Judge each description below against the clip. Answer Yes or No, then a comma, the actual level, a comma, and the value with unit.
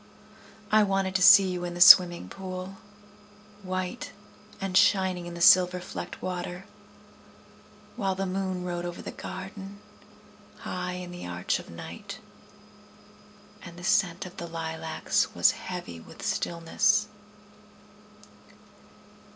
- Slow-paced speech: Yes, slow, 125 wpm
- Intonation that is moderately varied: No, narrow, 1.7 semitones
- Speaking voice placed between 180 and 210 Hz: Yes, medium, 185 Hz